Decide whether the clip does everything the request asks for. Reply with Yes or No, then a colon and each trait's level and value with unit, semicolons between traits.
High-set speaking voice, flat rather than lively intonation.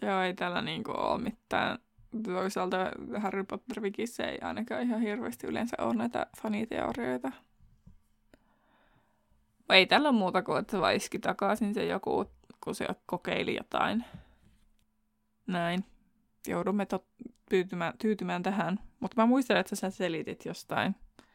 No: high, 195 Hz; average, 3.4 semitones